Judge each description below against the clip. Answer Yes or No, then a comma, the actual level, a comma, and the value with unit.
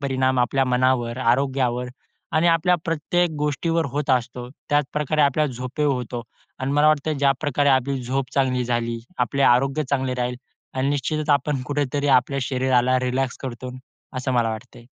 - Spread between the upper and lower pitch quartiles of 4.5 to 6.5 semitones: No, narrow, 2.5 semitones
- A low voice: Yes, low, 130 Hz